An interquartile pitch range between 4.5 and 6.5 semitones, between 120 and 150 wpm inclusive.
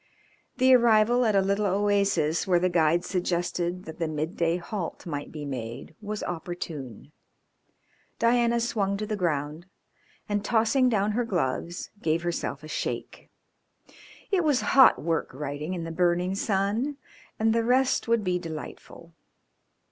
Yes: average, 4.9 semitones; average, 145 wpm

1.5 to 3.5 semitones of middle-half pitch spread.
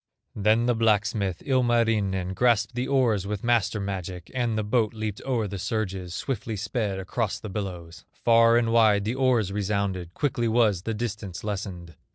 Yes: average, 3.2 semitones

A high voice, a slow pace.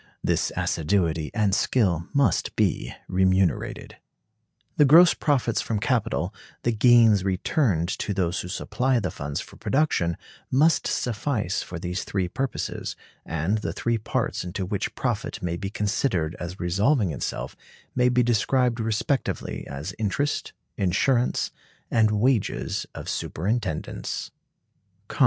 No: low, 105 Hz; slow, 125 wpm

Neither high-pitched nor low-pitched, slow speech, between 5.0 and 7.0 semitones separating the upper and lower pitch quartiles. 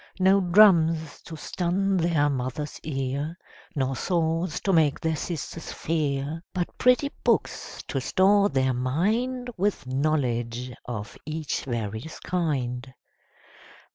Yes: medium, 155 Hz; slow, 115 wpm; wide, 5.4 semitones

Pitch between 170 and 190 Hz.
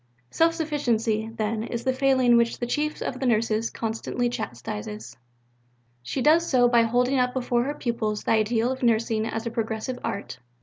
No: high, 235 Hz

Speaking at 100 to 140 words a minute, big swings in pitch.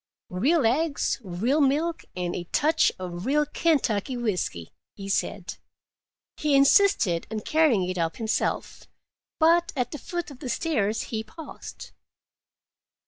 Yes: slow, 135 wpm; wide, 7.8 semitones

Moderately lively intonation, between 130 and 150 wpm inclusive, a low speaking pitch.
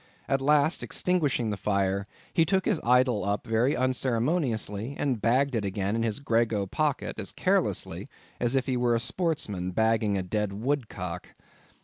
No: average, 4.9 semitones; average, 160 wpm; low, 115 Hz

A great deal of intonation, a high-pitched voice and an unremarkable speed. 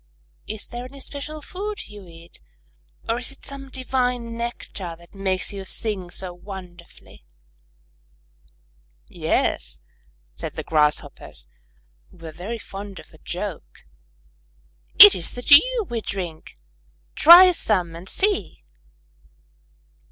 No: wide, 6.6 semitones; high, 205 Hz; slow, 120 wpm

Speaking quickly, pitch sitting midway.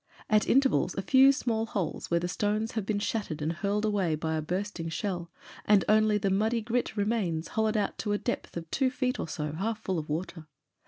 No: fast, 215 wpm; high, 205 Hz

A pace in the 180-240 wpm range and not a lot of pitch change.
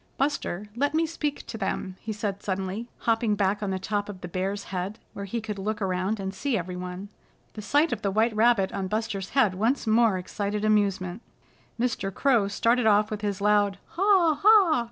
No: average, 195 wpm; average, 3.2 semitones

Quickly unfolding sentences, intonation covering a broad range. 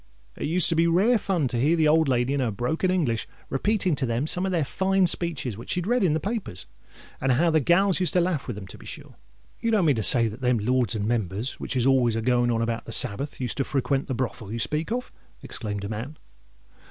Yes: fast, 250 wpm; wide, 6.7 semitones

